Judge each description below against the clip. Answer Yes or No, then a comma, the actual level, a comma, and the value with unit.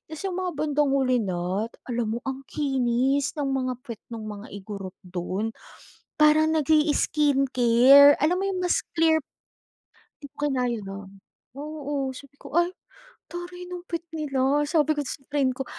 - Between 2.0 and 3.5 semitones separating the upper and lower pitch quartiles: No, average, 4.6 semitones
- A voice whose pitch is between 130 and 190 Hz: No, very high, 275 Hz